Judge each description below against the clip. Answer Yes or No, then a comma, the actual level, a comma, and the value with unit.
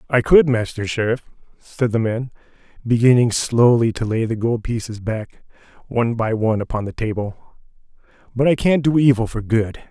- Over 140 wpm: Yes, average, 170 wpm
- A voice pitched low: Yes, low, 115 Hz